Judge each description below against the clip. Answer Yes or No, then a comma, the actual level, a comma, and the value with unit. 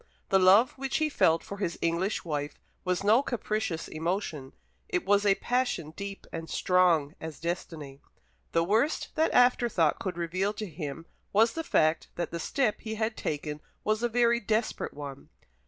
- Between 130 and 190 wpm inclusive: Yes, average, 170 wpm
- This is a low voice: No, medium, 185 Hz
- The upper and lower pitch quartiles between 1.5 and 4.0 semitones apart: No, average, 5.2 semitones